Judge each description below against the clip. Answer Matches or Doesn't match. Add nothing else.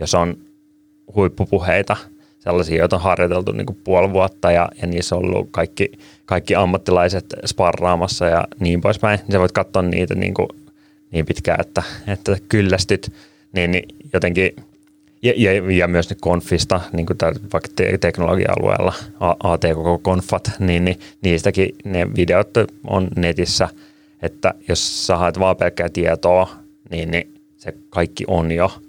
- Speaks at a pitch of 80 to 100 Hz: Matches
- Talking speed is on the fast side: Doesn't match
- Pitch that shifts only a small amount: Doesn't match